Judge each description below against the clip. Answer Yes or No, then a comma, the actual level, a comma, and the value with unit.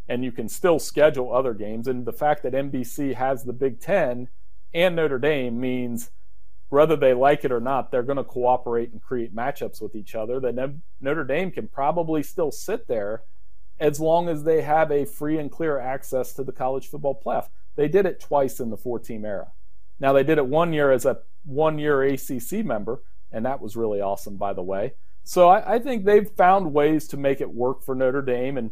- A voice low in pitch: Yes, low, 130 Hz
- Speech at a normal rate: No, fast, 210 wpm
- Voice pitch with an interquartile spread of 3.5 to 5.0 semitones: Yes, average, 4.0 semitones